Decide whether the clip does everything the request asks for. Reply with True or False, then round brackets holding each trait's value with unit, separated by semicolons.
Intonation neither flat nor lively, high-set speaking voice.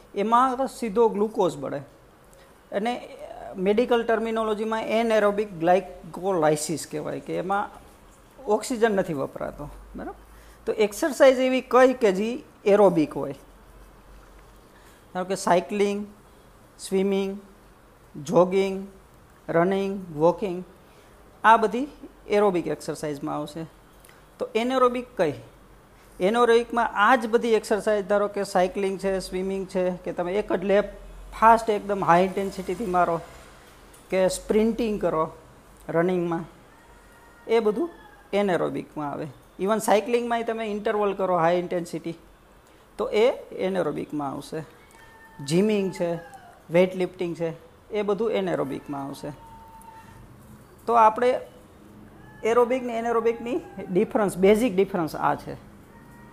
True (4.5 semitones; 200 Hz)